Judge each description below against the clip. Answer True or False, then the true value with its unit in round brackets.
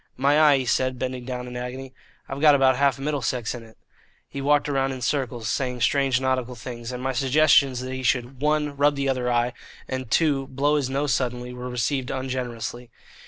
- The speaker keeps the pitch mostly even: True (1.9 semitones)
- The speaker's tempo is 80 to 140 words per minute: False (200 wpm)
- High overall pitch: False (130 Hz)